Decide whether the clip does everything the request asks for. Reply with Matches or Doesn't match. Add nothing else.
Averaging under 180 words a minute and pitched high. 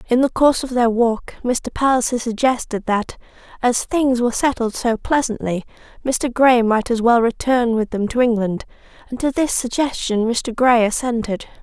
Matches